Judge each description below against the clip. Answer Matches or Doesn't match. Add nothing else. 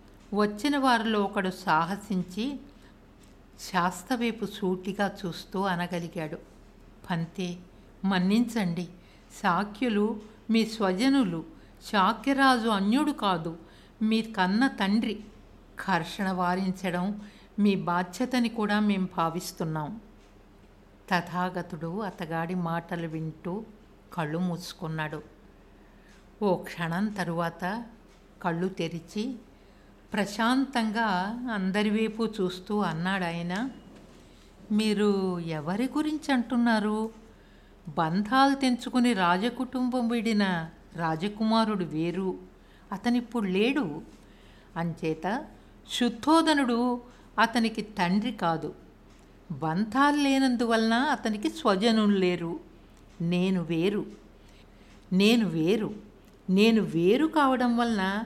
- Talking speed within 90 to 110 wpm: Doesn't match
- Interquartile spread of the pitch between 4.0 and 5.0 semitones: Matches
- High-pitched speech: Matches